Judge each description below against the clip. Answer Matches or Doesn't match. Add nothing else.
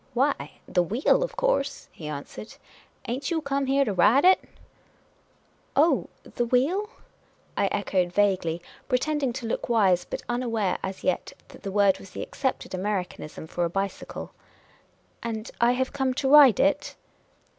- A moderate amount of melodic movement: Doesn't match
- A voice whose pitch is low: Doesn't match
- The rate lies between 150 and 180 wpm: Matches